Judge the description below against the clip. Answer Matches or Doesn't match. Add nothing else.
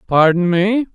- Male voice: Matches